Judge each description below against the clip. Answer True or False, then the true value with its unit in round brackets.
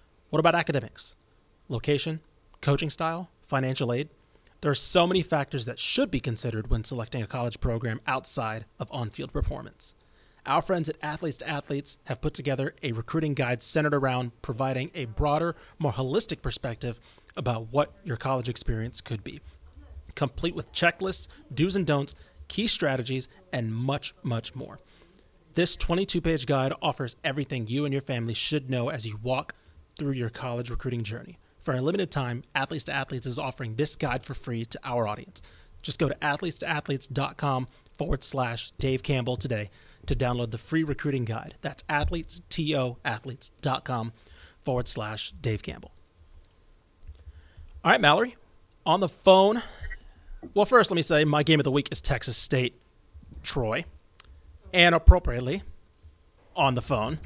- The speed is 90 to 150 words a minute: False (160 wpm)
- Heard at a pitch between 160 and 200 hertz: False (130 Hz)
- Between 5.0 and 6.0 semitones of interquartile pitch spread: False (4.5 semitones)